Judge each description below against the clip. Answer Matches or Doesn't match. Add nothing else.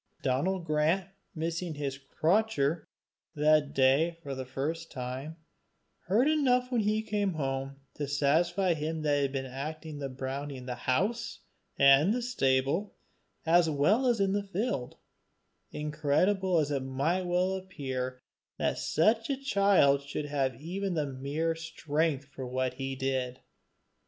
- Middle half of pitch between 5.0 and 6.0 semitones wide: Matches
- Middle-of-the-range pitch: Matches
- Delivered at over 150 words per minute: Doesn't match